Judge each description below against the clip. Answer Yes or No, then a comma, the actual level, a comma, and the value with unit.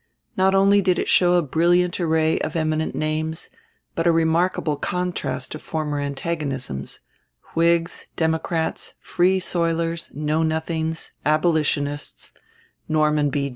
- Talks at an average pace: No, slow, 120 wpm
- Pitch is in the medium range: Yes, medium, 160 Hz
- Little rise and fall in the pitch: Yes, narrow, 1.9 semitones